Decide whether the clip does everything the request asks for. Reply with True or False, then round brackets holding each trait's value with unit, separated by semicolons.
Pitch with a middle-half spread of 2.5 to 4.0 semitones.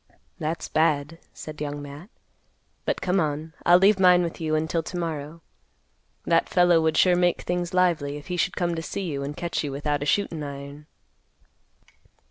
True (3.2 semitones)